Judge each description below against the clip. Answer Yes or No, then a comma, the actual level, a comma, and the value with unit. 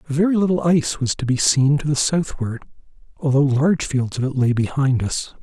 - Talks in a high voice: No, medium, 140 Hz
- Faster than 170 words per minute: Yes, average, 200 wpm